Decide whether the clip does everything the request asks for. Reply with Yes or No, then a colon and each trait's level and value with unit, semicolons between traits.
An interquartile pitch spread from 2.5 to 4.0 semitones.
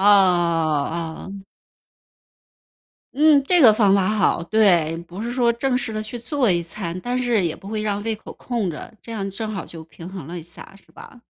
No: average, 5.1 semitones